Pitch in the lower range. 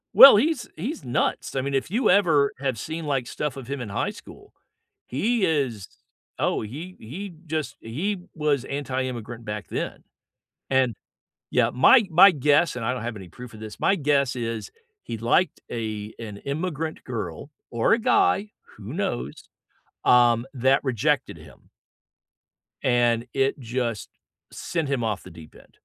Yes: low, 130 Hz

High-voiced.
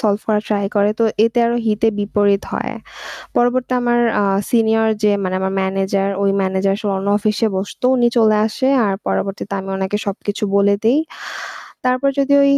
Yes: high, 210 Hz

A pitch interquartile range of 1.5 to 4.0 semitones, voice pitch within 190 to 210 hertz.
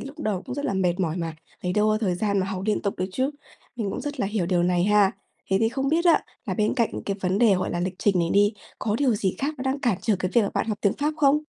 No: average, 5.2 semitones; high, 205 Hz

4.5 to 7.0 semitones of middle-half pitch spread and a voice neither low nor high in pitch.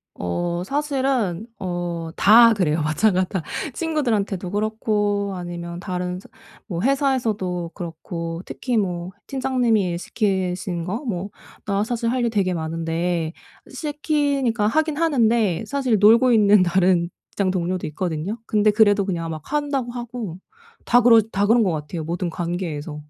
No: average, 5.1 semitones; high, 200 Hz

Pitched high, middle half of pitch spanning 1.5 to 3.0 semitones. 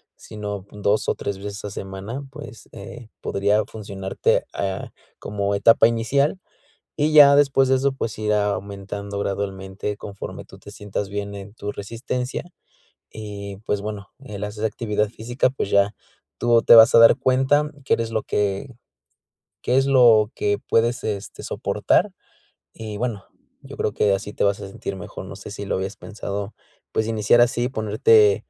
No: low, 105 Hz; narrow, 2.6 semitones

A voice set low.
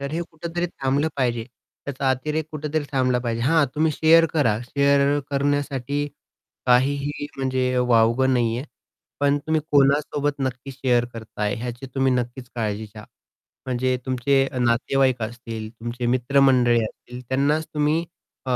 Yes: low, 130 Hz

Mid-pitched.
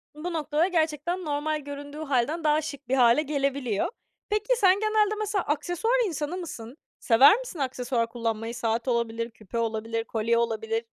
No: very high, 285 Hz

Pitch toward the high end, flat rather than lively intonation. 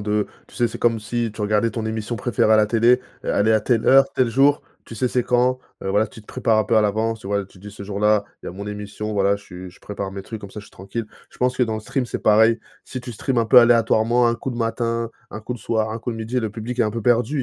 No: low, 110 Hz; narrow, 2.3 semitones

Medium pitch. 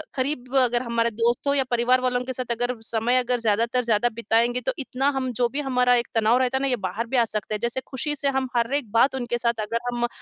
No: high, 245 Hz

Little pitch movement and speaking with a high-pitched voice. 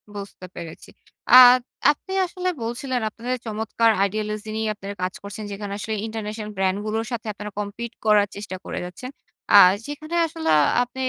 No: average, 3.0 semitones; high, 215 Hz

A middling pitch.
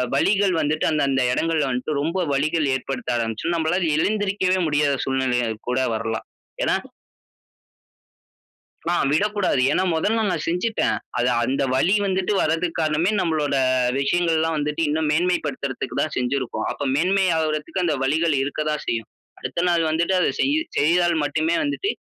Yes: medium, 160 Hz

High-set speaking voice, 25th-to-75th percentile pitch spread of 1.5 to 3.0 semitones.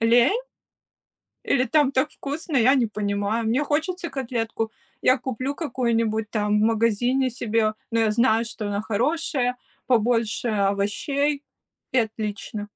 No: high, 235 Hz; average, 3.6 semitones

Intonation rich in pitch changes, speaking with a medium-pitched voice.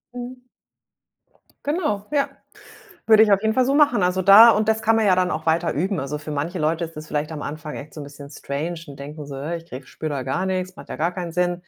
Yes: wide, 5.8 semitones; medium, 175 Hz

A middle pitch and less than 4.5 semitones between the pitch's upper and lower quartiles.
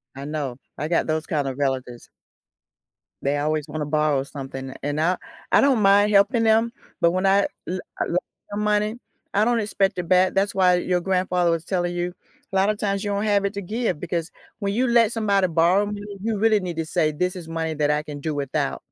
No: medium, 180 Hz; average, 4.8 semitones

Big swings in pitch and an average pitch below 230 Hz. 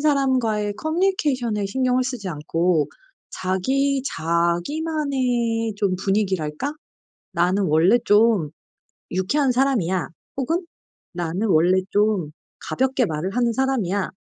Yes: wide, 6.5 semitones; high, 215 Hz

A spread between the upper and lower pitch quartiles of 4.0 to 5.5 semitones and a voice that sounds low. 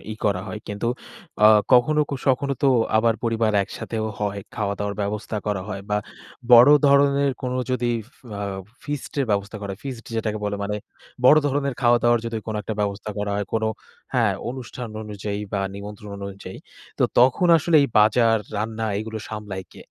No: average, 3.5 semitones; low, 110 Hz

